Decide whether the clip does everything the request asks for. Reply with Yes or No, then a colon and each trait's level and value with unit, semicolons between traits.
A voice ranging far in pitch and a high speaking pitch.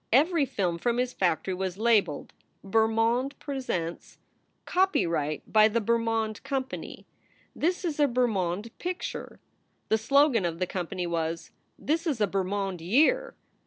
Yes: wide, 6.6 semitones; high, 220 Hz